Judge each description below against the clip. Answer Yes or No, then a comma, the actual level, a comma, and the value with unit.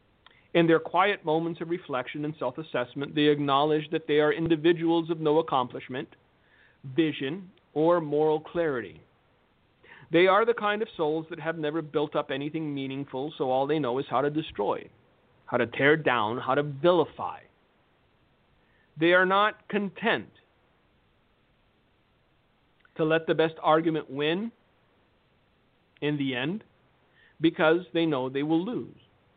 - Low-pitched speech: No, medium, 155 Hz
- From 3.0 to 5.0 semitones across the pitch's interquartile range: No, narrow, 2.5 semitones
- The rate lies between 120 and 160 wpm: Yes, average, 140 wpm